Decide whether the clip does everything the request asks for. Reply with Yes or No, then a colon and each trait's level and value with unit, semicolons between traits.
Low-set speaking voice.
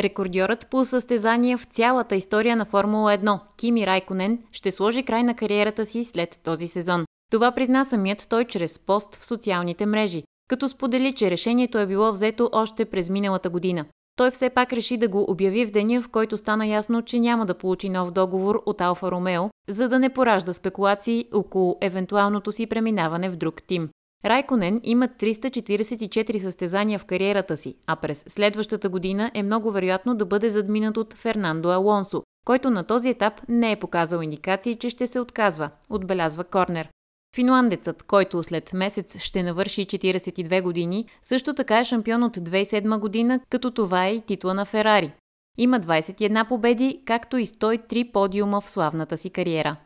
No: high, 210 Hz